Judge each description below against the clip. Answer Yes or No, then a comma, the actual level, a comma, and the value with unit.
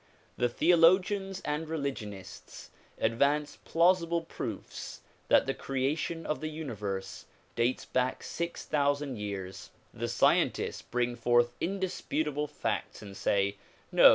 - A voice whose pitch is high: No, medium, 145 Hz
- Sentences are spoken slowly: Yes, slow, 125 wpm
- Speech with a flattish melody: No, wide, 5.6 semitones